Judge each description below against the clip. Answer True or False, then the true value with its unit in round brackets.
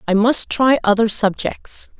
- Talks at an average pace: True (150 wpm)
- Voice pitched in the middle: False (225 Hz)